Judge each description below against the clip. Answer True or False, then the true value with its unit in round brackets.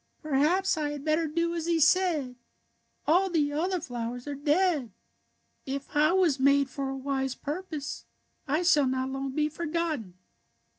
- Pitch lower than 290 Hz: False (295 Hz)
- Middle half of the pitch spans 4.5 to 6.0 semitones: False (3.9 semitones)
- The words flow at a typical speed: True (165 wpm)